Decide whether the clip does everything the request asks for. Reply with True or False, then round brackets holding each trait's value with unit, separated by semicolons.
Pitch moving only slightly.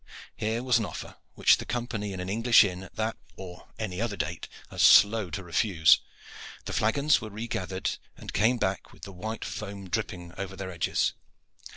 False (3.3 semitones)